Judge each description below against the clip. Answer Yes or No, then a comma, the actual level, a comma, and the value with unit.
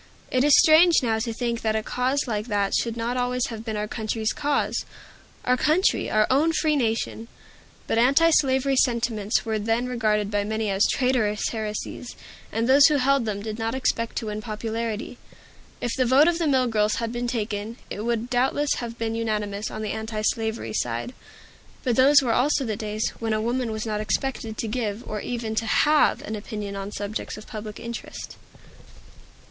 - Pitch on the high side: Yes, high, 230 Hz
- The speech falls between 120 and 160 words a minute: No, average, 185 wpm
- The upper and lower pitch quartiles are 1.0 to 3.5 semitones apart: Yes, average, 2.8 semitones